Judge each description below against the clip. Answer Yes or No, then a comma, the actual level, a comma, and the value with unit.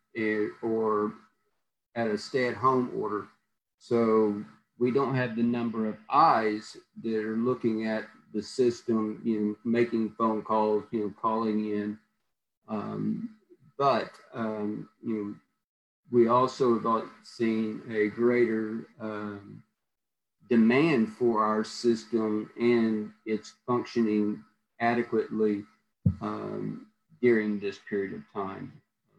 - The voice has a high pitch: No, low, 110 Hz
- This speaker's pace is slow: Yes, slow, 110 wpm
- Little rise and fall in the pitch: Yes, narrow, 1.8 semitones